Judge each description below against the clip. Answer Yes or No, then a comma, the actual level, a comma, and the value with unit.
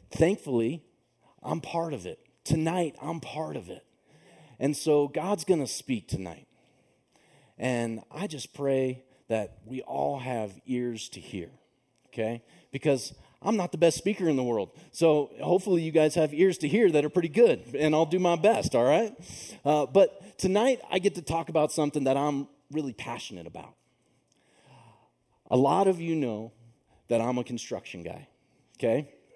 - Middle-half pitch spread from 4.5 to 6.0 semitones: Yes, average, 5.1 semitones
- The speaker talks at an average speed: Yes, average, 165 wpm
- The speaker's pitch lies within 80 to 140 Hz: No, medium, 150 Hz